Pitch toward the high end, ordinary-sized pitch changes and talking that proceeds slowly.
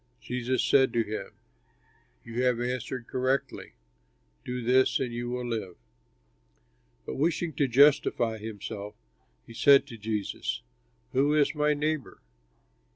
No: low, 125 Hz; average, 3.2 semitones; slow, 125 wpm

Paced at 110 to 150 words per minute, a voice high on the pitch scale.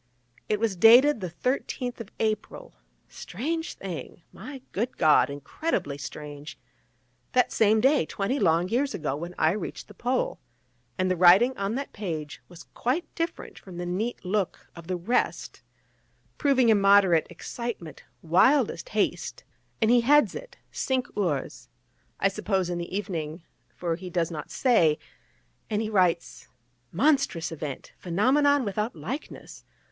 Yes: average, 140 wpm; high, 200 Hz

